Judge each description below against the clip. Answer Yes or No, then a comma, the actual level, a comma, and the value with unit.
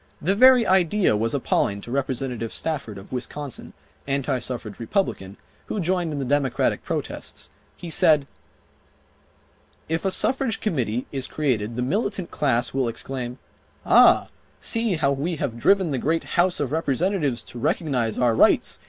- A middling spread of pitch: No, wide, 6.1 semitones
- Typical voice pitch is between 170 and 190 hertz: No, medium, 140 Hz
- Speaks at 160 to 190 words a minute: No, average, 150 wpm